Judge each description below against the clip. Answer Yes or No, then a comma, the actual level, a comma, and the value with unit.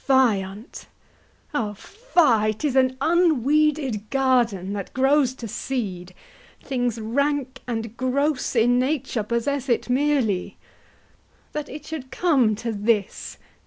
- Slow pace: Yes, slow, 120 wpm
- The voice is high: Yes, very high, 255 Hz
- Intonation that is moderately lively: Yes, average, 4.3 semitones